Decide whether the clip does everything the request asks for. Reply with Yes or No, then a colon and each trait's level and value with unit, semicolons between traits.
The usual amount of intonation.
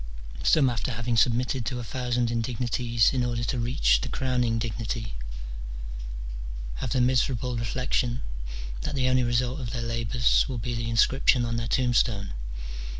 No: narrow, 1.5 semitones